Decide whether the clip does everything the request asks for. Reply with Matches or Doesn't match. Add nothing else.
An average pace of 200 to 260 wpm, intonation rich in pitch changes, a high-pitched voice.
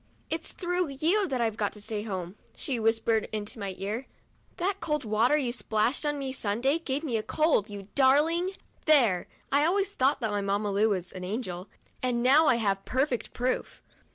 Matches